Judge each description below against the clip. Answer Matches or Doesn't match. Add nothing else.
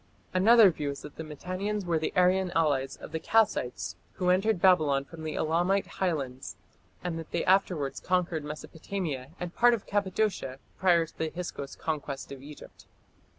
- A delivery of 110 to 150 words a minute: Doesn't match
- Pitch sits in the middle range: Matches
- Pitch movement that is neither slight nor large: Matches